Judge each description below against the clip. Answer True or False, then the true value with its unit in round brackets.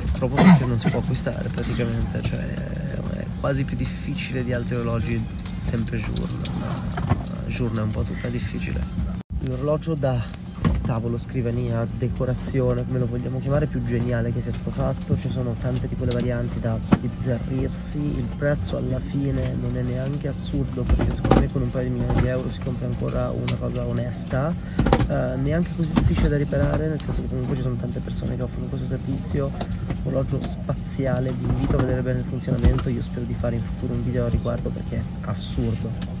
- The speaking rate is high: True (185 wpm)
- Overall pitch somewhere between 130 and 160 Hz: False (120 Hz)